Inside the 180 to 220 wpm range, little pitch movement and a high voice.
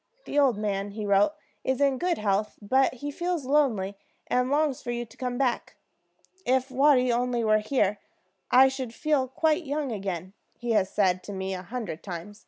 No: average, 190 wpm; average, 4.8 semitones; high, 245 Hz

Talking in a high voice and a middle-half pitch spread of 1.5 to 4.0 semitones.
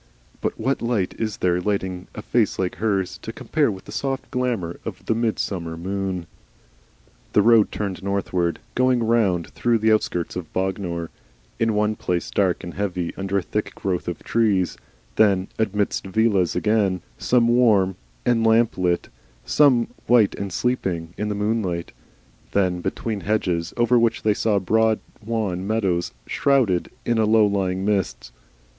No: low, 100 Hz; average, 3.5 semitones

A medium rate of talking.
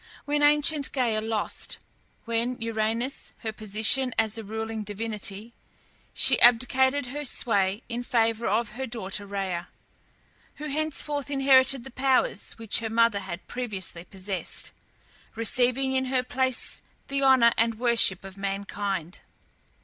No: slow, 130 wpm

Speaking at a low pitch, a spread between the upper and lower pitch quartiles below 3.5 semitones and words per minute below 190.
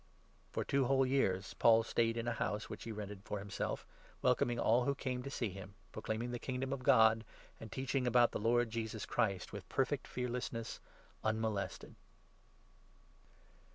Yes: low, 115 Hz; narrow, 2.6 semitones; average, 170 wpm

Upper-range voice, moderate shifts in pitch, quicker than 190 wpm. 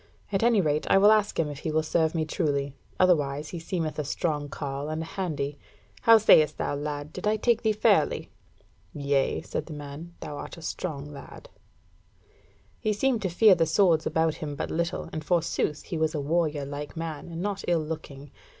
No: medium, 160 Hz; average, 3.4 semitones; average, 200 wpm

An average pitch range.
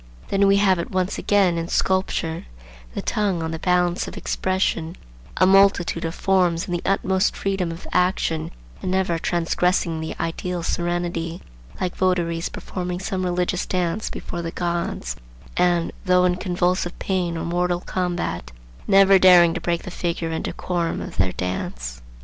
No: narrow, 1.9 semitones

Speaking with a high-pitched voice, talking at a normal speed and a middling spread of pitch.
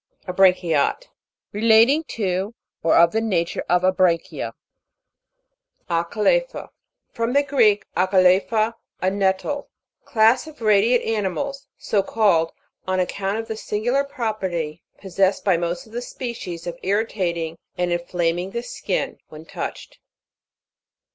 No: high, 195 Hz; slow, 120 wpm; average, 4.5 semitones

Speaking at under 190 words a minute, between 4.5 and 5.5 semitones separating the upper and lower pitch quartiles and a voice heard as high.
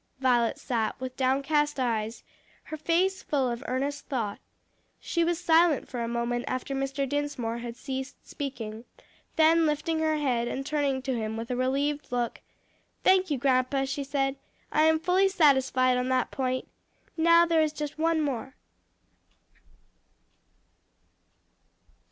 No: average, 145 wpm; average, 3.5 semitones; very high, 275 Hz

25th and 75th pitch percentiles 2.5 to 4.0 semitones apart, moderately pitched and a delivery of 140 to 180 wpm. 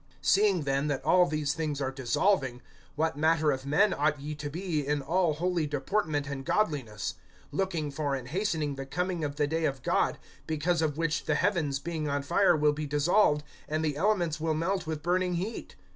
No: average, 3.4 semitones; medium, 155 Hz; average, 195 wpm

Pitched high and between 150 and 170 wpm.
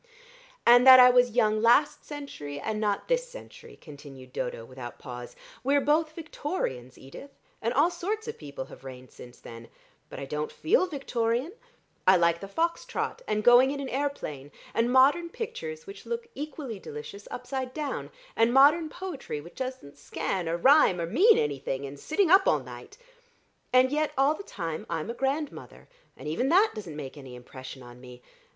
No: high, 245 Hz; average, 180 wpm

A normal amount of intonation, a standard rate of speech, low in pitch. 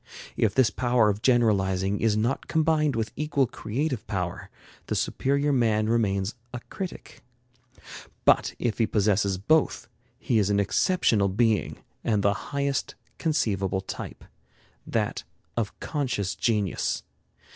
No: average, 4.8 semitones; slow, 125 wpm; low, 110 Hz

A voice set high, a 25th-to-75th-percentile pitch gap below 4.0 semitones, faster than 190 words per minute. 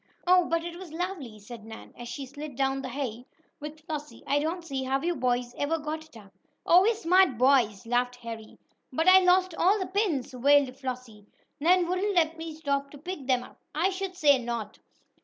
No: very high, 290 Hz; wide, 5.5 semitones; fast, 205 wpm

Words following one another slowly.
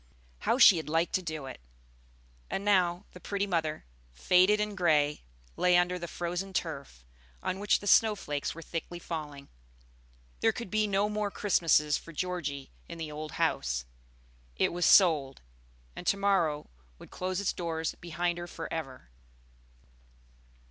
No: average, 155 wpm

